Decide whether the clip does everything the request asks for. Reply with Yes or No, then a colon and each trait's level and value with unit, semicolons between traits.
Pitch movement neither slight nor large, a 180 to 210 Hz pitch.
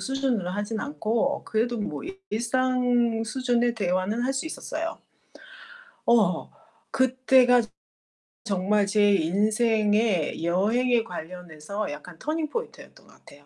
No: average, 4.0 semitones; high, 225 Hz